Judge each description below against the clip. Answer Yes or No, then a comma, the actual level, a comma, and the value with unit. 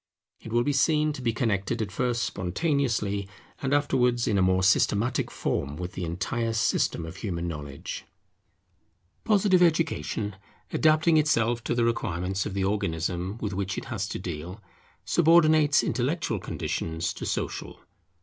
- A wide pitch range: Yes, wide, 7.1 semitones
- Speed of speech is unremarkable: Yes, average, 150 wpm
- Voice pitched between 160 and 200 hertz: No, low, 110 Hz